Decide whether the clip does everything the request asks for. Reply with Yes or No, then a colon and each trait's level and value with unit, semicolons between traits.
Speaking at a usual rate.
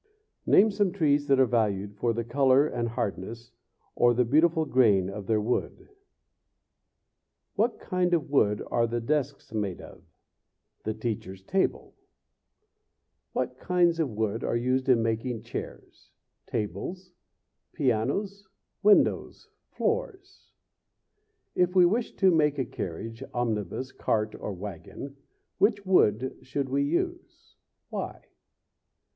No: slow, 125 wpm